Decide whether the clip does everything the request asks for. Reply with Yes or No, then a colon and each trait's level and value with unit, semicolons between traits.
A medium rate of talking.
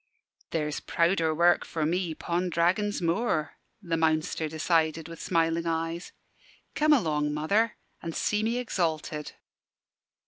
No: slow, 125 wpm